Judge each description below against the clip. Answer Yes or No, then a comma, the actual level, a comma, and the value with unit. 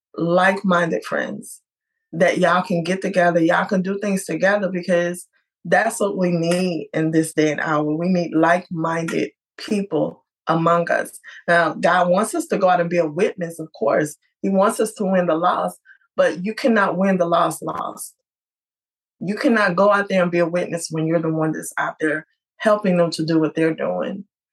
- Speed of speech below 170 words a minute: No, average, 190 wpm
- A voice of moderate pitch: Yes, medium, 175 Hz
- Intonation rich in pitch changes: No, average, 2.9 semitones